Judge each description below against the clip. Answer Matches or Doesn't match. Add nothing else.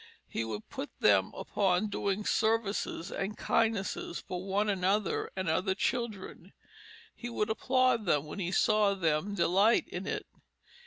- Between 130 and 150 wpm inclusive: Matches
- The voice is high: Matches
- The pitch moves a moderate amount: Matches